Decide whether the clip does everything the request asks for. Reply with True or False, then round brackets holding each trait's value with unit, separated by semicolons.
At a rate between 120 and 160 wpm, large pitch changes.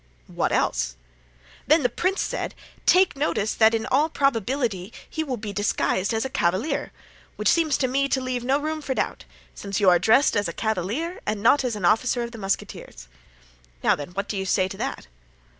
False (195 wpm; 5.7 semitones)